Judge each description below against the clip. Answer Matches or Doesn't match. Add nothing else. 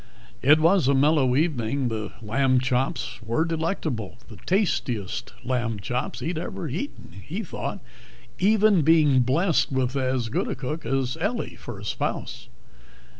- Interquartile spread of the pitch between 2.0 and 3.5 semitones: Doesn't match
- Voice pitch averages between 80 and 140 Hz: Matches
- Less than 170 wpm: Matches